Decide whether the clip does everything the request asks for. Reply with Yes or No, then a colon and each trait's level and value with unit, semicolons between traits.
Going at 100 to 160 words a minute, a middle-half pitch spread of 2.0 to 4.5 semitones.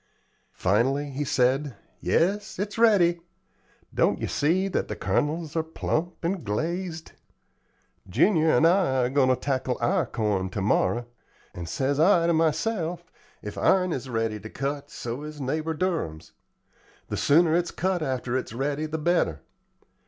No: average, 150 wpm; average, 5.3 semitones